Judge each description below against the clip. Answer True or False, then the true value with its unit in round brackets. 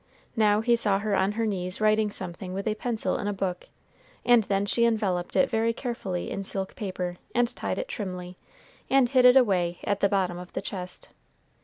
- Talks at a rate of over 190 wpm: True (200 wpm)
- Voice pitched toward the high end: True (205 Hz)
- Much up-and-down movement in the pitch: False (3.7 semitones)